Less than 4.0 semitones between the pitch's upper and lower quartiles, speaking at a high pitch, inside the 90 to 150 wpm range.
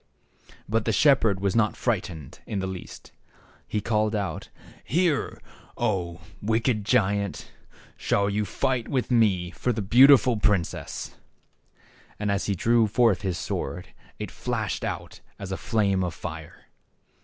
No: average, 3.3 semitones; low, 105 Hz; average, 145 wpm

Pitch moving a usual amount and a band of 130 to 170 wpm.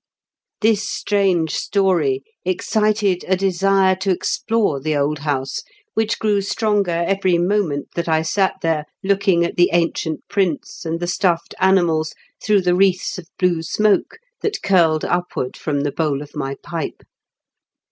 Yes: average, 3.6 semitones; average, 145 wpm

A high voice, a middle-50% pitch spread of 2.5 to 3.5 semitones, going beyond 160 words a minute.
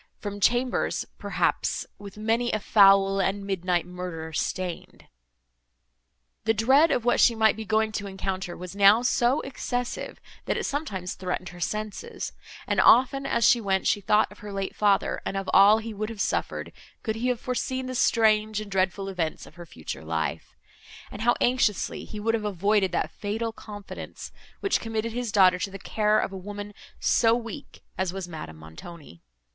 Yes: high, 205 Hz; average, 3.0 semitones; average, 180 wpm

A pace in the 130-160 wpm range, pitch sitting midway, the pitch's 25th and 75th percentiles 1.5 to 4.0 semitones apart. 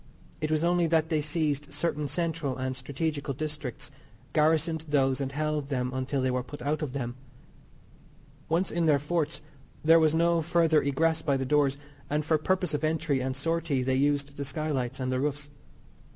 No: average, 180 wpm; medium, 150 Hz; average, 2.9 semitones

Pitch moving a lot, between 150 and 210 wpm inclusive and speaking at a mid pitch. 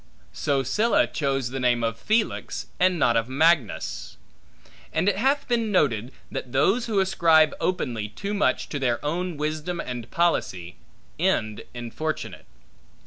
No: wide, 7.3 semitones; average, 140 wpm; medium, 150 Hz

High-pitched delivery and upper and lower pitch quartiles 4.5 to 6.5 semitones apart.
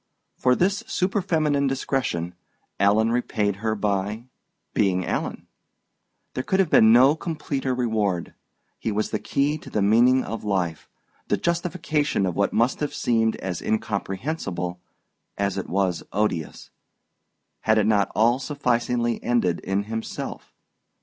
No: low, 110 Hz; average, 5.2 semitones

